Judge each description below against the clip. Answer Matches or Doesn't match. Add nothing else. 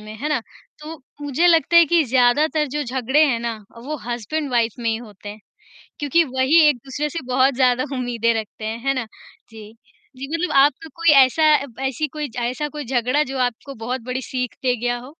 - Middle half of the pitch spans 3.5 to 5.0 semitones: Matches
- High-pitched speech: Matches